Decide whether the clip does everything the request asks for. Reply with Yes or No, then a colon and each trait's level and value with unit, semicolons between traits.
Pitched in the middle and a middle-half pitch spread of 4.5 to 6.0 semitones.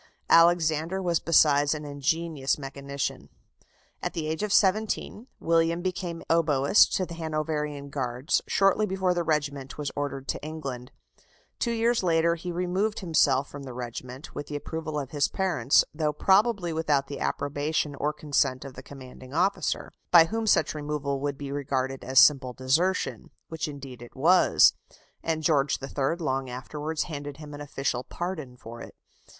No: medium, 150 Hz; average, 3.4 semitones